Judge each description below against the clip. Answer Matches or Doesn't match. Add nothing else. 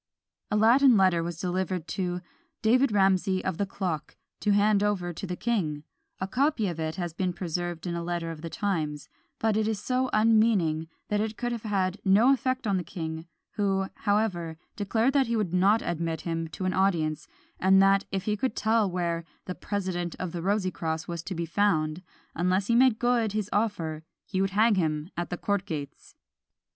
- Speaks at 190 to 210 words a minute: Matches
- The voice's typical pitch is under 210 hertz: Matches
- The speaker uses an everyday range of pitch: Matches